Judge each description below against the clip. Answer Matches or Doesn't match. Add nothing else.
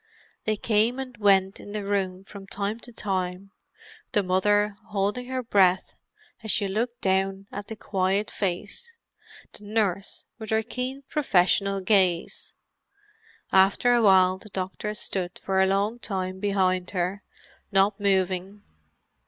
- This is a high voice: Matches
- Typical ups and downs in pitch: Doesn't match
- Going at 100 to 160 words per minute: Matches